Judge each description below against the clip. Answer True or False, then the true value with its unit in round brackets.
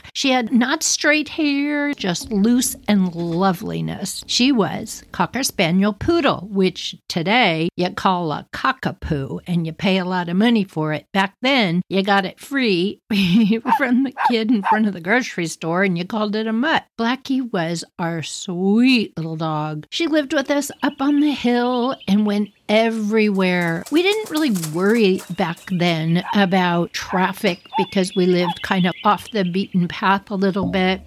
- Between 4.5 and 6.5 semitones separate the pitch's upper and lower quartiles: True (5.3 semitones)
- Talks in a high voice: True (200 Hz)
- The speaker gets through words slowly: False (170 wpm)